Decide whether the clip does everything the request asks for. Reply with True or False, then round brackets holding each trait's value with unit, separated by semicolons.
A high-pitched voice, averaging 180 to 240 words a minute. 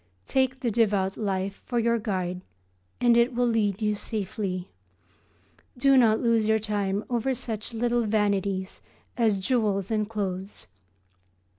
False (215 Hz; 135 wpm)